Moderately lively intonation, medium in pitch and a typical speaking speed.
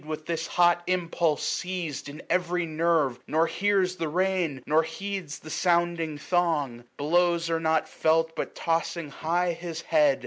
No: narrow, 2.1 semitones; medium, 165 Hz; average, 160 wpm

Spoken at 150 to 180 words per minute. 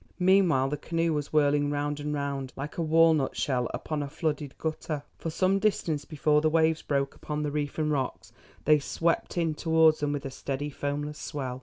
No: average, 195 wpm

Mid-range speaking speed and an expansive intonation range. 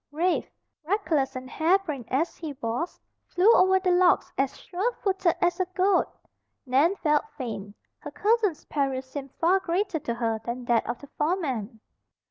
Yes: average, 160 wpm; wide, 6.2 semitones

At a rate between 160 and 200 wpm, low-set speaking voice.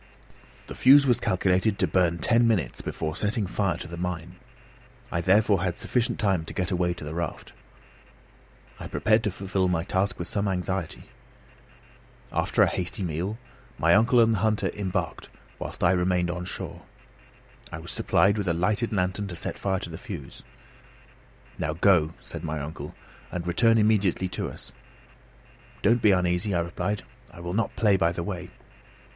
Yes: average, 175 wpm; very low, 95 Hz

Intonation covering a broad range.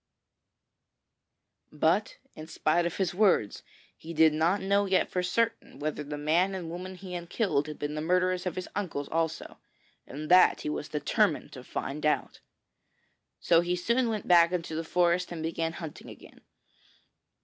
No: average, 2.9 semitones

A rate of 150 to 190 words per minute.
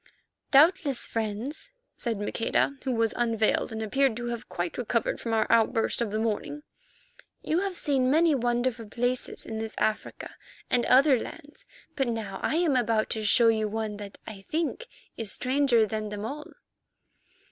Yes: average, 165 wpm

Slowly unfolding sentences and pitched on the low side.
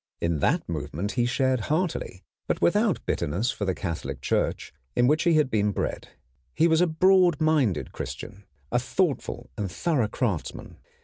No: average, 165 wpm; low, 120 Hz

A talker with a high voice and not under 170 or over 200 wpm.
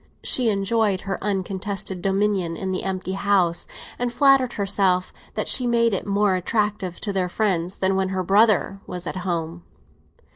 No: high, 195 Hz; average, 160 wpm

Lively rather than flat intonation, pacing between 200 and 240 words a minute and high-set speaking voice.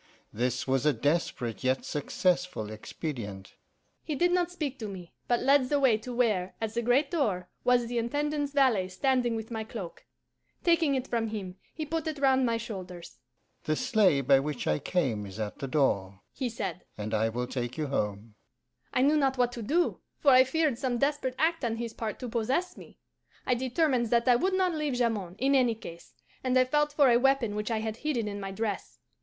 Yes: wide, 7.6 semitones; fast, 205 wpm; high, 230 Hz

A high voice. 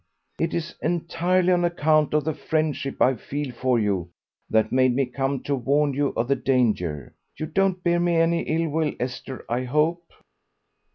No: medium, 145 Hz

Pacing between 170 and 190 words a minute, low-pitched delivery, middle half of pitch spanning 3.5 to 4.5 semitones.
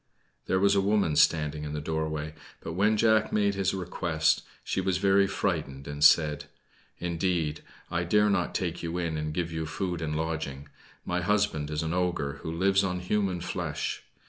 Yes: average, 180 wpm; very low, 85 Hz; average, 3.8 semitones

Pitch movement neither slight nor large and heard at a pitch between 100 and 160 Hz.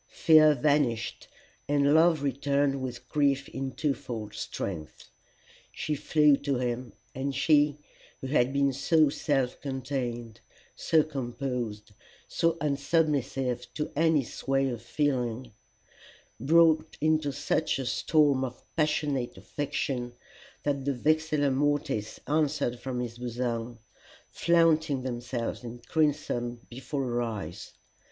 Yes: average, 3.5 semitones; low, 135 Hz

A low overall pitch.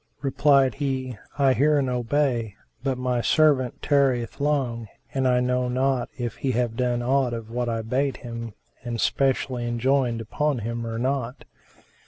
Yes: low, 125 Hz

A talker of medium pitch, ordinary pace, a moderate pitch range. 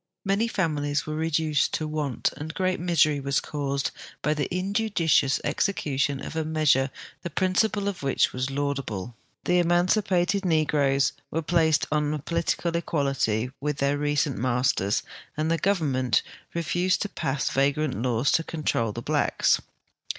Yes: medium, 150 Hz; average, 150 wpm; average, 3.7 semitones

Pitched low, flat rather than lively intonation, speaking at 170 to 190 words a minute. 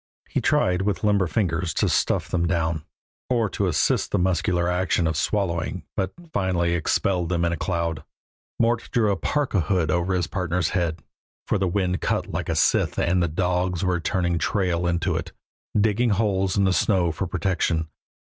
Yes: very low, 90 Hz; narrow, 2.2 semitones; average, 180 wpm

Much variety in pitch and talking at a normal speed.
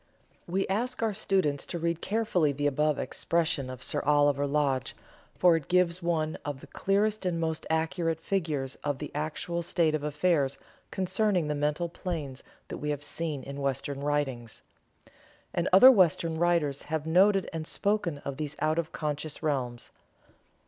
No: average, 3.3 semitones; average, 160 wpm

